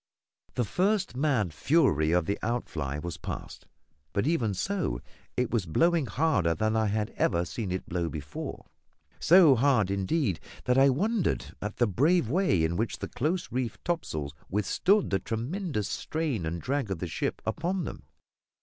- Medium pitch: No, low, 115 Hz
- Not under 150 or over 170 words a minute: Yes, average, 165 wpm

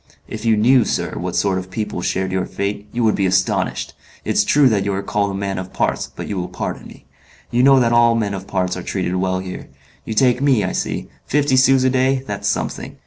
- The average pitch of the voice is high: No, low, 105 Hz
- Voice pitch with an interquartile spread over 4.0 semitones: Yes, average, 4.9 semitones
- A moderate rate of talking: No, fast, 240 wpm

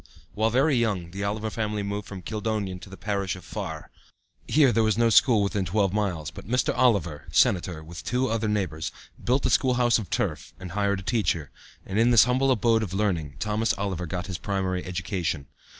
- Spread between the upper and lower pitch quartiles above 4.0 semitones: No, average, 3.7 semitones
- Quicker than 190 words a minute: Yes, average, 200 wpm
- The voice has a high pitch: No, low, 100 Hz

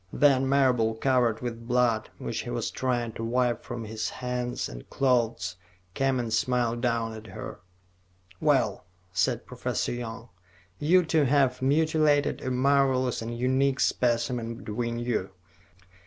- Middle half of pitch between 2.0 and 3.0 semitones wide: Yes, narrow, 2.5 semitones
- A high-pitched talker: No, low, 125 Hz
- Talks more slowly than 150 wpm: Yes, average, 140 wpm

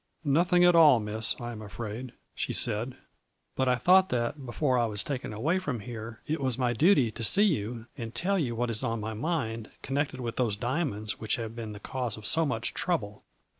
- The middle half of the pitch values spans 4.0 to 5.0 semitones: Yes, average, 4.6 semitones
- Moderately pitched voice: No, low, 120 Hz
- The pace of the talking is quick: Yes, fast, 220 wpm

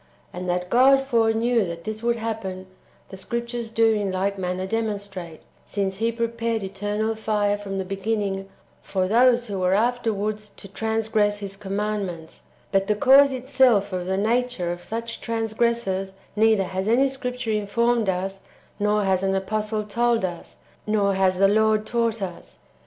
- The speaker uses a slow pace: No, average, 160 wpm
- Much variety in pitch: No, average, 3.0 semitones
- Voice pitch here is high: Yes, high, 210 Hz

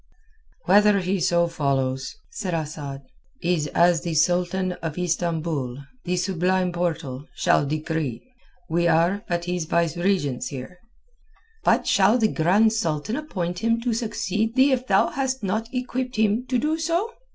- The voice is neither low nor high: Yes, medium, 180 Hz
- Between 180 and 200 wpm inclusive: No, average, 145 wpm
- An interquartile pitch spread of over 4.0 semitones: Yes, average, 5.2 semitones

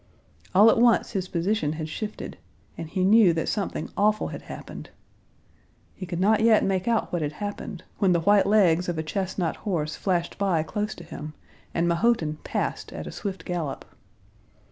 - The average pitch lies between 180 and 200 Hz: Yes, medium, 185 Hz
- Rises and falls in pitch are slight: No, average, 3.9 semitones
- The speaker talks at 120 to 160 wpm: No, average, 180 wpm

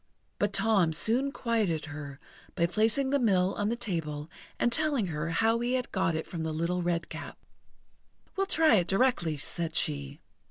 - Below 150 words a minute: No, average, 170 wpm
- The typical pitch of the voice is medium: Yes, medium, 180 Hz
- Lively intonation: Yes, wide, 6.4 semitones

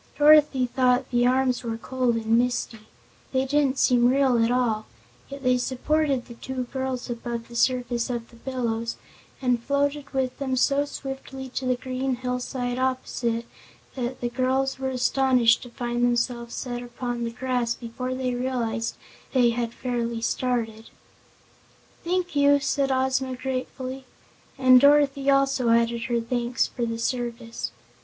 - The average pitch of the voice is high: Yes, very high, 250 Hz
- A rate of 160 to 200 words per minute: No, average, 150 wpm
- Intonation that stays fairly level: Yes, narrow, 1.9 semitones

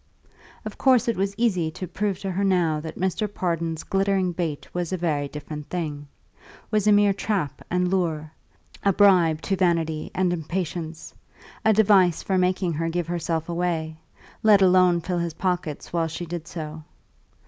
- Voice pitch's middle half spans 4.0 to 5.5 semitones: No, average, 2.9 semitones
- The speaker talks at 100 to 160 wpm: No, average, 170 wpm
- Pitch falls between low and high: Yes, medium, 175 Hz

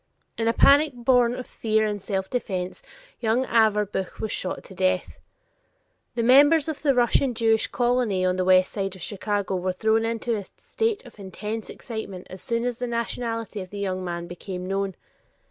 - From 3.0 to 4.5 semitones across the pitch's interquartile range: Yes, average, 4.1 semitones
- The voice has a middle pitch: No, high, 220 Hz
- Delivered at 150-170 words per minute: No, average, 180 wpm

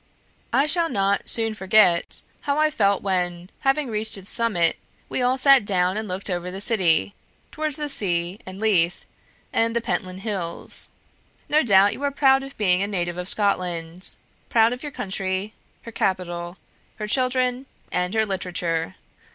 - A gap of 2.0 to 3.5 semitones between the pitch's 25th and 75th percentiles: No, average, 5.2 semitones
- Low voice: No, high, 200 Hz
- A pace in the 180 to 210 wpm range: No, average, 165 wpm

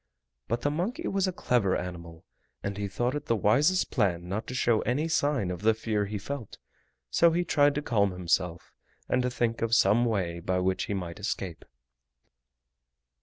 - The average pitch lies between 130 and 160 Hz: No, low, 110 Hz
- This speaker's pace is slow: No, average, 185 wpm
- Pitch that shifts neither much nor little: No, wide, 7.1 semitones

